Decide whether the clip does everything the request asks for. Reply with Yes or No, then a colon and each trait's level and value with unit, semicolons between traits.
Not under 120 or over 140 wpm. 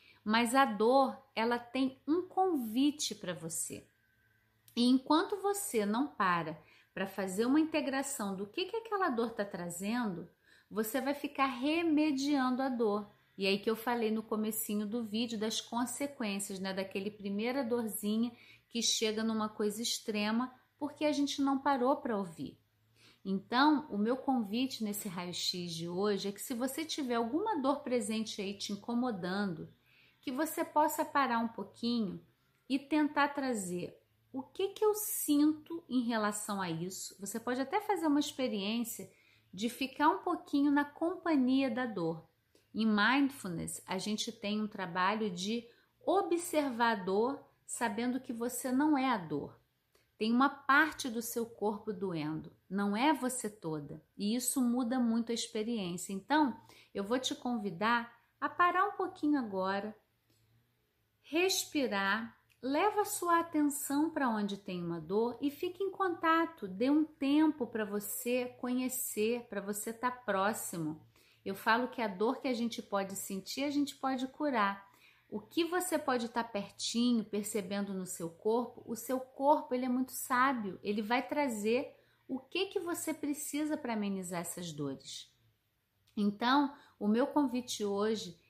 No: average, 155 wpm